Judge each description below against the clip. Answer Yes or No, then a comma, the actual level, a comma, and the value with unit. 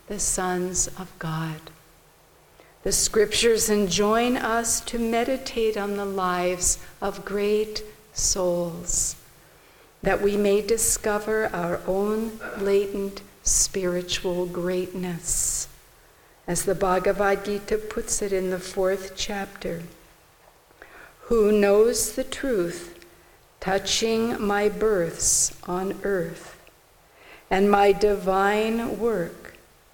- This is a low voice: No, high, 200 Hz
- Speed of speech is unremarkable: No, slow, 95 wpm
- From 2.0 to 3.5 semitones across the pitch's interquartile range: Yes, average, 2.9 semitones